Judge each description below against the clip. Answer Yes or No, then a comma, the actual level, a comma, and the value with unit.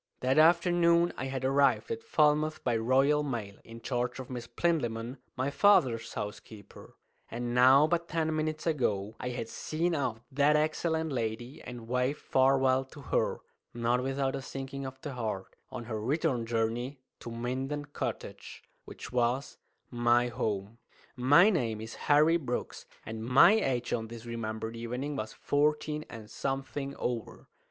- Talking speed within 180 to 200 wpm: No, average, 155 wpm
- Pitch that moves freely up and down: No, average, 4.0 semitones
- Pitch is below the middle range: Yes, low, 130 Hz